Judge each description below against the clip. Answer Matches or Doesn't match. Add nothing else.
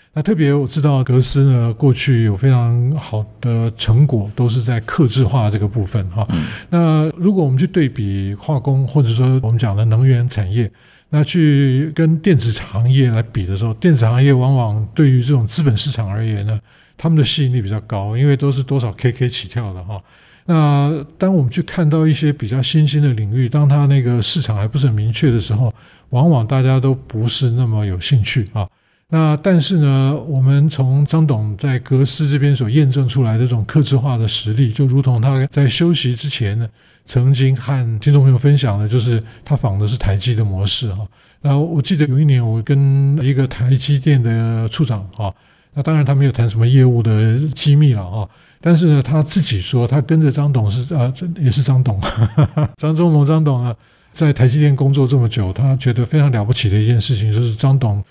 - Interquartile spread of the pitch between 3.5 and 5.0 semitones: Matches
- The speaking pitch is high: Doesn't match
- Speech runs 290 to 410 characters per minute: Matches